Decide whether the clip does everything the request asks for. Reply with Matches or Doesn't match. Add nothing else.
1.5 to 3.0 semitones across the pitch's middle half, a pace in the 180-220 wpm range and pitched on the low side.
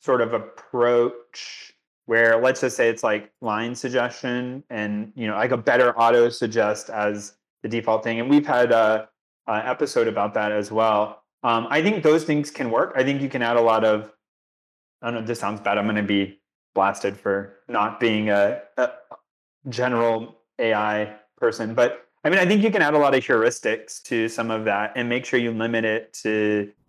Matches